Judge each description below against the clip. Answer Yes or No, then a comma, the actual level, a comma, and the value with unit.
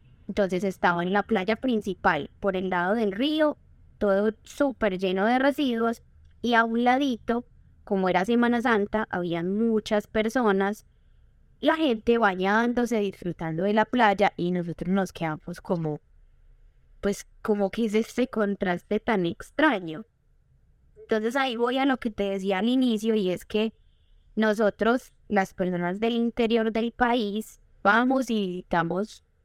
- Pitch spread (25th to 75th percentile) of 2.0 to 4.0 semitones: Yes, average, 3.4 semitones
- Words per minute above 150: No, average, 145 wpm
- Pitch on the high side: Yes, high, 215 Hz